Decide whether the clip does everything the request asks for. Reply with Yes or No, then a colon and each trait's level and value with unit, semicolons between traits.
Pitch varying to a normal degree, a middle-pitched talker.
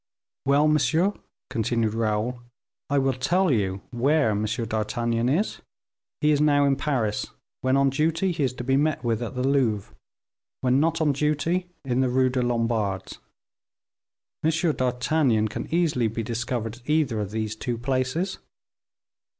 No: average, 4.5 semitones; low, 130 Hz